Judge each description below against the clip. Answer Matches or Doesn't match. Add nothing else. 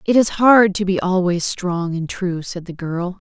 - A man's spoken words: Doesn't match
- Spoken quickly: Matches